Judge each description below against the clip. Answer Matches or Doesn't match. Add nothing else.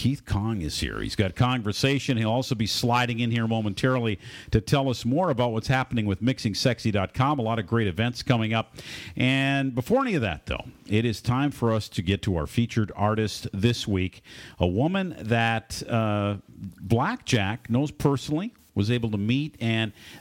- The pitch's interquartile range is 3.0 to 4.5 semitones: Matches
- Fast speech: Doesn't match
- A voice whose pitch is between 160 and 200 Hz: Doesn't match